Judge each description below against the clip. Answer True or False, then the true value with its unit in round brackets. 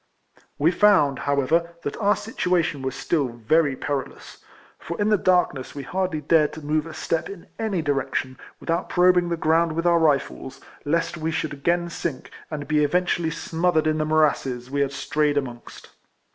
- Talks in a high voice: False (155 Hz)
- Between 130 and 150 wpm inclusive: False (175 wpm)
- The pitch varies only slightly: False (3.3 semitones)